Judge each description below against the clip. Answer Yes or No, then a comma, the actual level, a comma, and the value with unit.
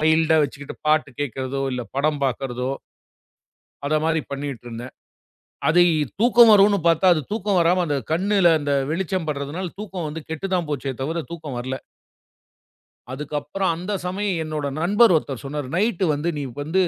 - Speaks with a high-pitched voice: No, medium, 160 Hz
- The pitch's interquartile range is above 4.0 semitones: Yes, average, 4.5 semitones